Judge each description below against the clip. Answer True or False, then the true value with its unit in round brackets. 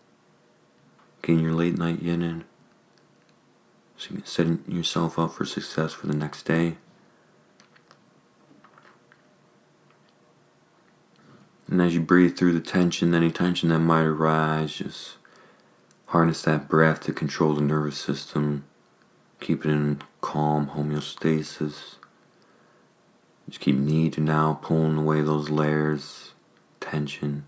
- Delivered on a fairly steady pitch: True (1.6 semitones)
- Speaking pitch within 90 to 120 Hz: False (80 Hz)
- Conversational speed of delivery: False (115 wpm)